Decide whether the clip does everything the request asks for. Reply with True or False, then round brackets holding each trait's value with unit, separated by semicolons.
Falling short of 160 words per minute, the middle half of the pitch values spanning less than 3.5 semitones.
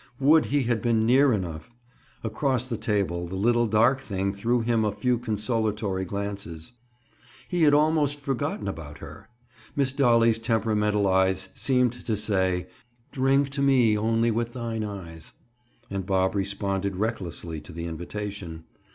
False (145 wpm; 4.1 semitones)